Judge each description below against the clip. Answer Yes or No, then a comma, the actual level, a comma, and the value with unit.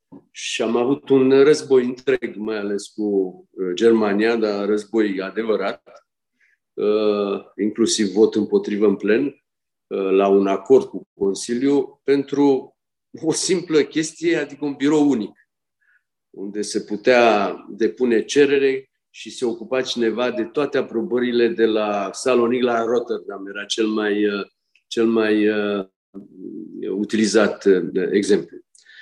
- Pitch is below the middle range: Yes, low, 110 Hz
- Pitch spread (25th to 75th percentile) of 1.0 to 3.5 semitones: No, average, 4.1 semitones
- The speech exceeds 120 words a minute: No, slow, 115 wpm